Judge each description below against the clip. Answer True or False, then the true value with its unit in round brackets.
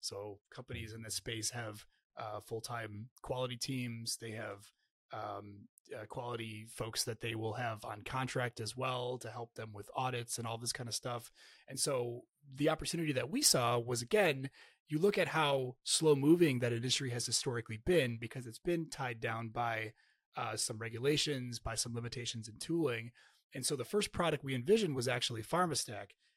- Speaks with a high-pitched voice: False (120 Hz)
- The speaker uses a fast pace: False (180 wpm)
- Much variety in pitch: False (3.4 semitones)